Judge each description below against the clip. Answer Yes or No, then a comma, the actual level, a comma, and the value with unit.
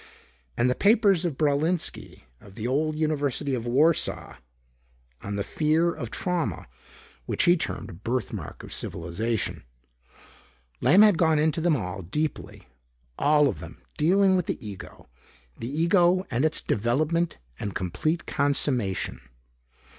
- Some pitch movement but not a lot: No, wide, 6.1 semitones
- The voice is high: No, medium, 150 Hz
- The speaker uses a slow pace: Yes, slow, 130 wpm